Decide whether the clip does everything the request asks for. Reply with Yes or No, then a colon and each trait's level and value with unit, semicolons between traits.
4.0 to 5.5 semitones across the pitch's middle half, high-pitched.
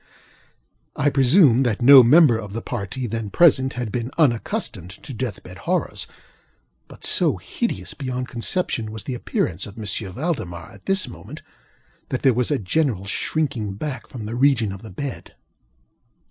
No: average, 4.3 semitones; low, 120 Hz